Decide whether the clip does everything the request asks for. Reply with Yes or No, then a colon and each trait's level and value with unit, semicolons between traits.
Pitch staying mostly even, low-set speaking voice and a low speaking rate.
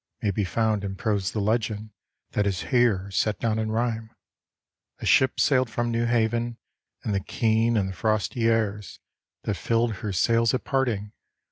No: narrow, 2.3 semitones; low, 110 Hz; average, 170 wpm